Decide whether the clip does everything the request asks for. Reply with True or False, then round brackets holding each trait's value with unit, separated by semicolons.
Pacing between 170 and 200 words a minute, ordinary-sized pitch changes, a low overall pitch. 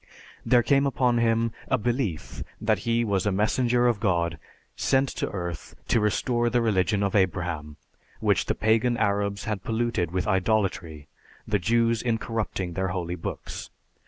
False (160 wpm; 4.1 semitones; 105 Hz)